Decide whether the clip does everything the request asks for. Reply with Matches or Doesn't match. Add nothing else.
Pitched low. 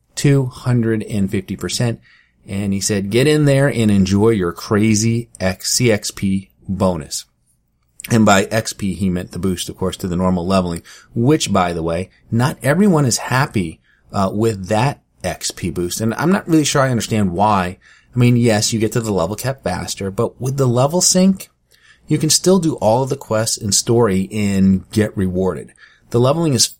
Matches